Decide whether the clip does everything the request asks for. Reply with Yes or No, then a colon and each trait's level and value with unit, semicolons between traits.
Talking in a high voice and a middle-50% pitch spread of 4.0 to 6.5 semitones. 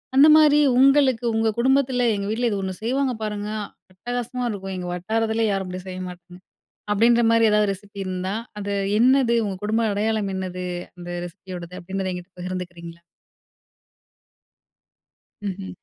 Yes: high, 205 Hz; average, 4.3 semitones